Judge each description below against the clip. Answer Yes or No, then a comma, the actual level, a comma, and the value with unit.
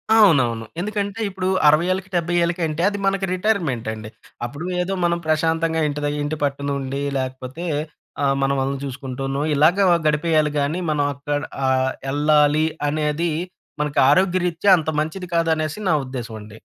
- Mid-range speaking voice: Yes, medium, 150 Hz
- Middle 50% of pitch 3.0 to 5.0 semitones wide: Yes, average, 3.8 semitones